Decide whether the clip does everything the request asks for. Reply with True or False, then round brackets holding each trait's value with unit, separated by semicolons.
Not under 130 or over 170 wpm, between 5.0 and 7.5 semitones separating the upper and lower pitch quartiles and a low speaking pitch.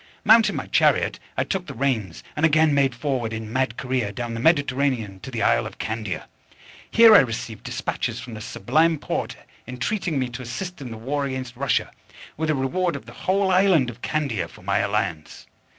False (195 wpm; 5.4 semitones; 130 Hz)